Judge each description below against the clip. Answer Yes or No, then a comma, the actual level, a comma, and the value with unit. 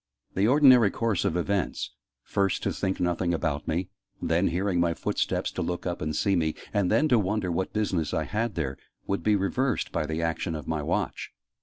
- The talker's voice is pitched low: Yes, very low, 90 Hz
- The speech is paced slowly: No, average, 200 wpm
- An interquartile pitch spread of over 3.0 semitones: Yes, average, 3.7 semitones